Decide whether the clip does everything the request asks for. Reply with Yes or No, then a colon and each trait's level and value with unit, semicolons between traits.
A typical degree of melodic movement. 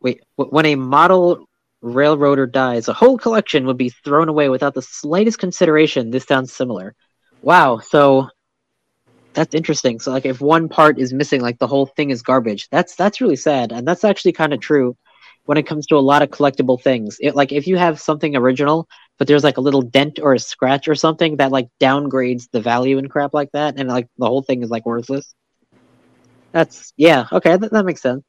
Yes: average, 3.0 semitones